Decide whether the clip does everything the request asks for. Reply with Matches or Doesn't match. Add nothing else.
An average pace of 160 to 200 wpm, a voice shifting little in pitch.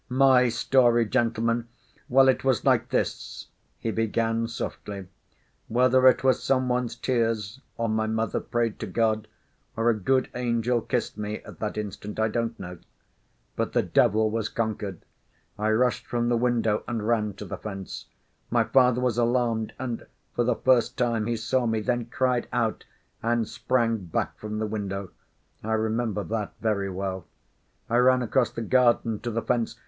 Matches